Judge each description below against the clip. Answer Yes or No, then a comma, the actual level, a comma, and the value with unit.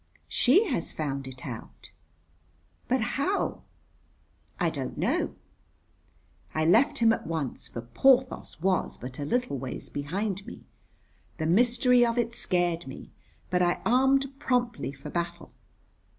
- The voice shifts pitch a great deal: Yes, wide, 8.6 semitones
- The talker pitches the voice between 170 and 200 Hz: Yes, medium, 185 Hz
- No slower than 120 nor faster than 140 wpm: Yes, slow, 135 wpm